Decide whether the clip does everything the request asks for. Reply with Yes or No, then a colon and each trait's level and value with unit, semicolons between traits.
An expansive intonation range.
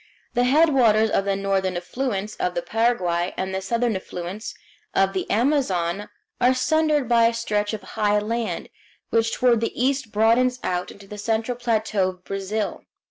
No: average, 3.8 semitones